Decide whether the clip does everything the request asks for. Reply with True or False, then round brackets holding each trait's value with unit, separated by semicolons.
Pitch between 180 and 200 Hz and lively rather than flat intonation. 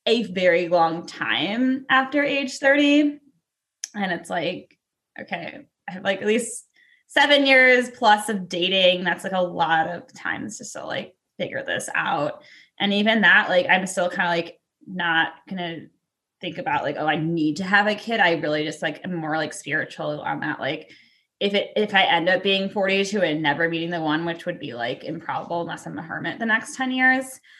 True (190 Hz; 5.7 semitones)